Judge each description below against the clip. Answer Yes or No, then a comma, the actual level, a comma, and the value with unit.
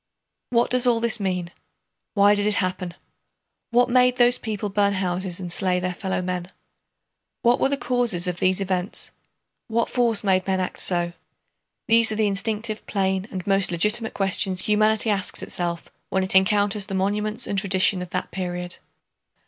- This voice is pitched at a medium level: No, high, 195 Hz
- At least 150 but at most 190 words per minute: Yes, average, 170 wpm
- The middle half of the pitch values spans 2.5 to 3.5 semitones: Yes, average, 3.0 semitones